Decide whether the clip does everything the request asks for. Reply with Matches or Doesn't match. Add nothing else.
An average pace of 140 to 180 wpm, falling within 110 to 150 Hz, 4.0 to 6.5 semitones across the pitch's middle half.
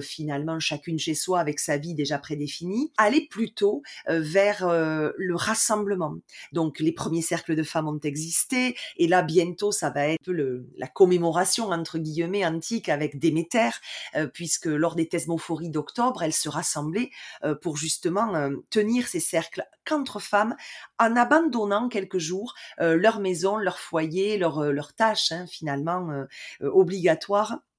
Doesn't match